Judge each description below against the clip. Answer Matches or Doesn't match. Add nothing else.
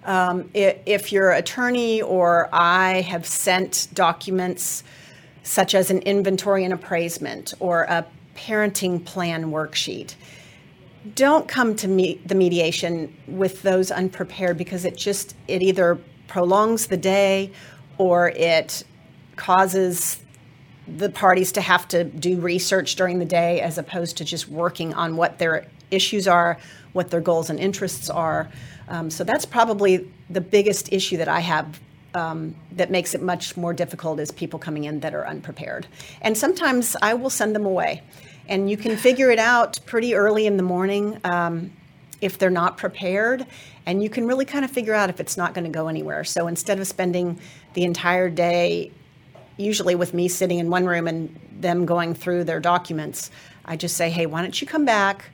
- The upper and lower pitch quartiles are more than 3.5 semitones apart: Doesn't match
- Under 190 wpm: Matches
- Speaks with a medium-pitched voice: Matches